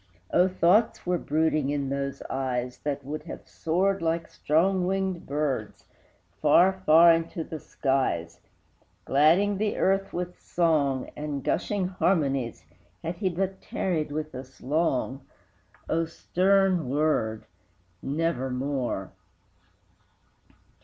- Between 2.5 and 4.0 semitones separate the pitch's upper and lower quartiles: No, average, 4.6 semitones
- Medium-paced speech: No, slow, 110 wpm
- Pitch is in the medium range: Yes, medium, 155 Hz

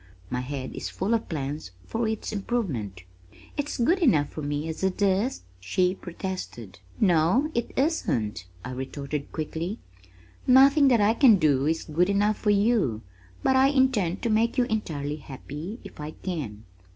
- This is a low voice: No, medium, 185 Hz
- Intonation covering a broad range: Yes, wide, 8.0 semitones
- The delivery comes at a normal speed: Yes, average, 165 wpm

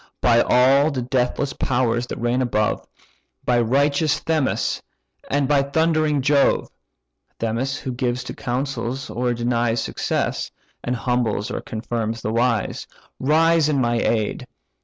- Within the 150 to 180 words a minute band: No, slow, 135 wpm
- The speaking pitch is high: No, low, 125 Hz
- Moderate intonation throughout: Yes, average, 3.0 semitones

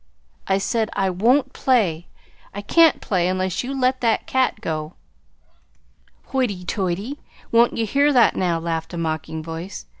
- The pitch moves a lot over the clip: Yes, wide, 6.6 semitones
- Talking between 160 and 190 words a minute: No, average, 150 wpm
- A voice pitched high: Yes, high, 195 Hz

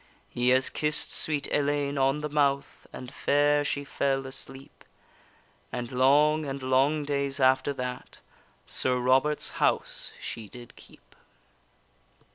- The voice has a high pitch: No, medium, 140 Hz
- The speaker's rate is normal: No, slow, 125 wpm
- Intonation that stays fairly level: Yes, narrow, 2.0 semitones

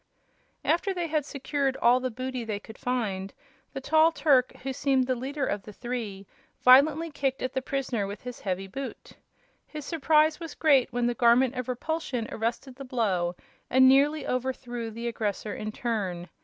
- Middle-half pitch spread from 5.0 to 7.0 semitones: No, average, 3.4 semitones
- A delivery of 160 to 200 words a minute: Yes, average, 175 wpm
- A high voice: Yes, very high, 255 Hz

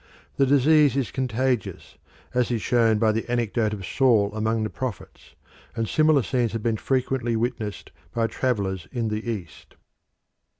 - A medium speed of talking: Yes, average, 155 wpm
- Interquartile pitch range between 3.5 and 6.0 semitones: No, average, 3.0 semitones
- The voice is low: Yes, low, 115 Hz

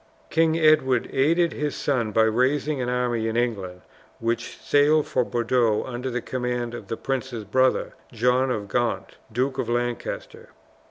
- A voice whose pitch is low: Yes, low, 125 Hz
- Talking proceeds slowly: No, average, 155 wpm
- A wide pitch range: No, narrow, 2.4 semitones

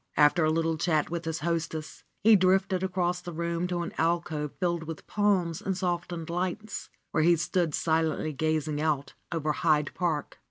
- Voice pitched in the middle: Yes, medium, 170 Hz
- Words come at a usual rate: Yes, average, 170 wpm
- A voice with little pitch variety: Yes, narrow, 2.1 semitones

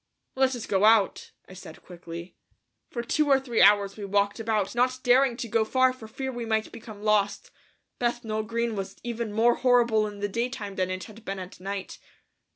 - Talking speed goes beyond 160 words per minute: Yes, average, 195 wpm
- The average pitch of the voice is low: No, high, 220 Hz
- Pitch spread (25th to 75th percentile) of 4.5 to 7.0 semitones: No, average, 3.1 semitones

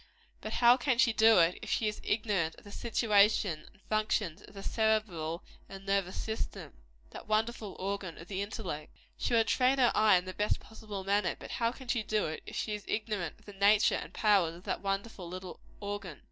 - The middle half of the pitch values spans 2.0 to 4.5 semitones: Yes, average, 2.8 semitones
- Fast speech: Yes, fast, 210 wpm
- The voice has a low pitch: No, high, 205 Hz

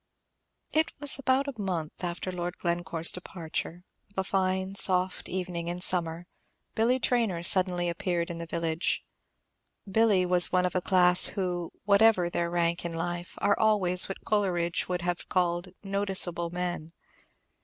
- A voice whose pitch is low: No, medium, 180 Hz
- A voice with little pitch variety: Yes, narrow, 2.0 semitones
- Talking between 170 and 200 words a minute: No, average, 150 wpm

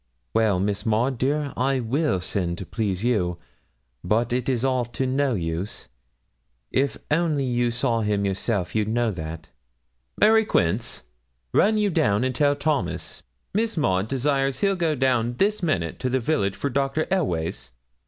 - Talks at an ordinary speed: Yes, average, 160 wpm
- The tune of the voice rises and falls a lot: Yes, wide, 5.7 semitones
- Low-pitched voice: Yes, low, 120 Hz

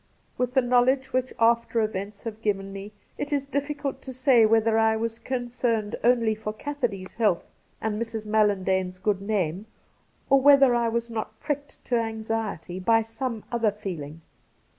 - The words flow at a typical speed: Yes, average, 170 wpm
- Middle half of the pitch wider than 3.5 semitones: No, average, 2.9 semitones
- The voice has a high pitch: Yes, high, 225 Hz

